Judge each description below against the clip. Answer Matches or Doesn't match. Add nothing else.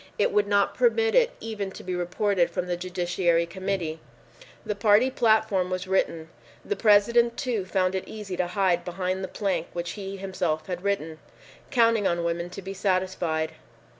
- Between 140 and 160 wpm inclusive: Doesn't match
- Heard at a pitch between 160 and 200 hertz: Matches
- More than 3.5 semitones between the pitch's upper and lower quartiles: Doesn't match